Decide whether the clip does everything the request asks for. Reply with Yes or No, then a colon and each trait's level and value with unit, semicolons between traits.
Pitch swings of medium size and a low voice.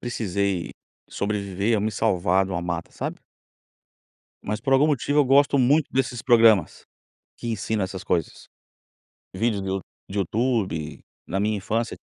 Yes: average, 4.1 semitones; low, 105 Hz